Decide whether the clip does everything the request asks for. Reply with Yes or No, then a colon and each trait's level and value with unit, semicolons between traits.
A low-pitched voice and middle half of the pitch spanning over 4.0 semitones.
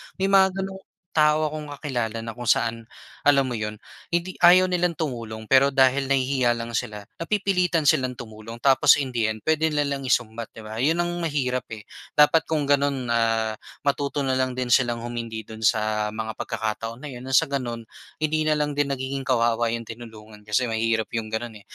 Yes: low, 130 Hz; average, 4.4 semitones